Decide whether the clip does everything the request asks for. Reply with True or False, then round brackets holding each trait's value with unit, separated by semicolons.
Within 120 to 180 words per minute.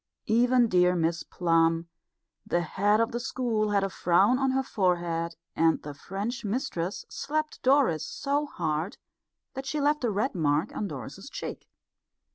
True (155 wpm)